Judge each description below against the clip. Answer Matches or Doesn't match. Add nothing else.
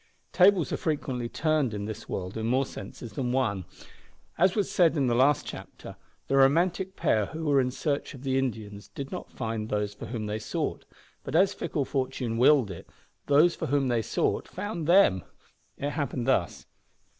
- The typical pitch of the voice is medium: Doesn't match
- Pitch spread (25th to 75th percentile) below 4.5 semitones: Doesn't match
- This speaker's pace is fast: Doesn't match